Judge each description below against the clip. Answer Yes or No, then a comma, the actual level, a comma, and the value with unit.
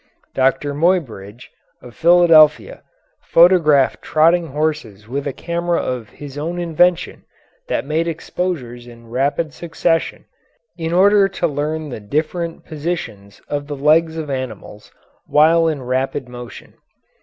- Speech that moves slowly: Yes, slow, 125 wpm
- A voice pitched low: No, medium, 150 Hz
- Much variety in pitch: No, average, 4.4 semitones